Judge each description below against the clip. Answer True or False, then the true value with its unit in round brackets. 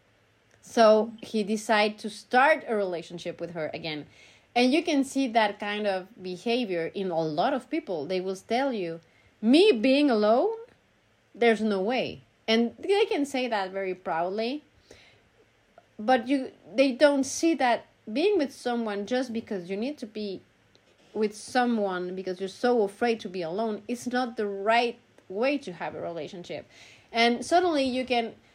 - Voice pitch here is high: True (225 Hz)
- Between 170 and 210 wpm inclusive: False (160 wpm)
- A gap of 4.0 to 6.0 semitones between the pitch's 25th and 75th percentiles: True (5.1 semitones)